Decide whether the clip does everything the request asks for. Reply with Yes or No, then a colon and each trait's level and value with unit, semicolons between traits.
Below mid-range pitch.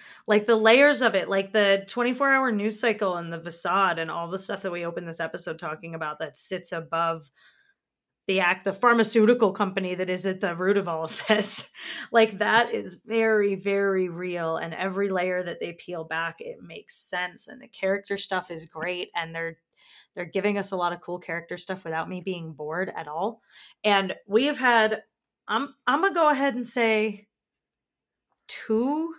No: high, 195 Hz